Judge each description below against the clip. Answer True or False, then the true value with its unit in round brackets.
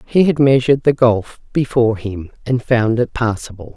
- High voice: False (120 Hz)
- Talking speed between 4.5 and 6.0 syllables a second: True (5.1 syllables/s)